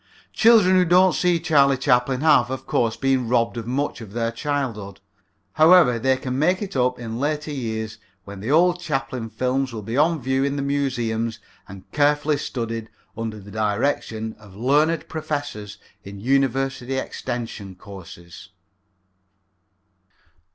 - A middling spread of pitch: Yes, average, 4.5 semitones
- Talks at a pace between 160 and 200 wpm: No, average, 145 wpm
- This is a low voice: Yes, low, 130 Hz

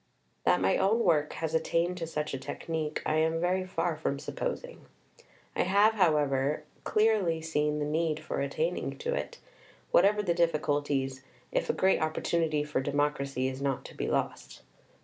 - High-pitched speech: No, medium, 160 Hz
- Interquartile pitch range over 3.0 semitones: Yes, average, 3.6 semitones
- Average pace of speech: Yes, average, 165 wpm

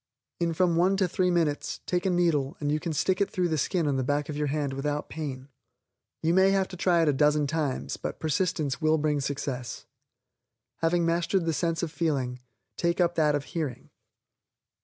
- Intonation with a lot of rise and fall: No, average, 3.1 semitones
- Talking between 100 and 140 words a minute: No, average, 200 wpm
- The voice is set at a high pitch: No, medium, 160 Hz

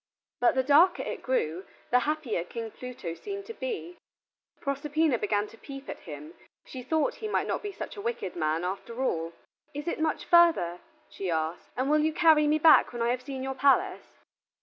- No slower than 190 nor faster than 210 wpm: Yes, average, 195 wpm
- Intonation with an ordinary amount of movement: No, wide, 7.4 semitones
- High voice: Yes, very high, 265 Hz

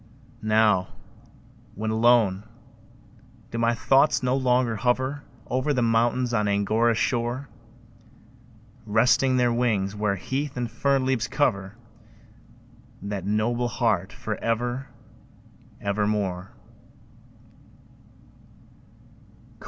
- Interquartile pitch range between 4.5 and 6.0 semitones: No, average, 3.1 semitones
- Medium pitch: No, low, 115 Hz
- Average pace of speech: No, slow, 95 wpm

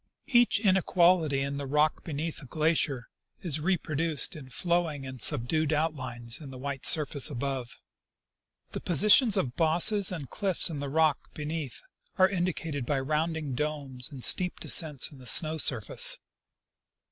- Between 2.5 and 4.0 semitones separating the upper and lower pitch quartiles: Yes, average, 3.5 semitones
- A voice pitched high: No, medium, 150 Hz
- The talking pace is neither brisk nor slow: Yes, average, 150 wpm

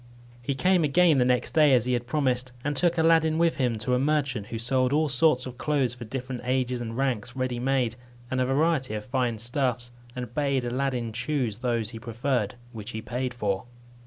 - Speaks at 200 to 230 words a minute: Yes, fast, 205 wpm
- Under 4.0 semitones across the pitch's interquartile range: Yes, narrow, 2.5 semitones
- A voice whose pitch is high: No, low, 125 Hz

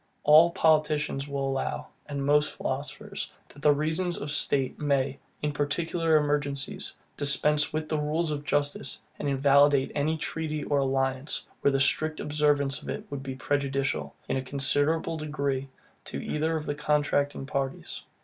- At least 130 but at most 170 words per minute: Yes, average, 150 wpm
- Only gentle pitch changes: Yes, narrow, 1.7 semitones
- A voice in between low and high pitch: Yes, medium, 145 Hz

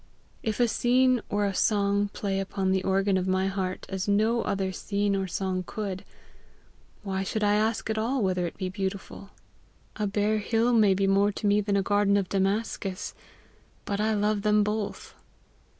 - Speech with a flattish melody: Yes, narrow, 1.7 semitones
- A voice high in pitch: Yes, high, 200 Hz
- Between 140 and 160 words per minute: No, average, 180 wpm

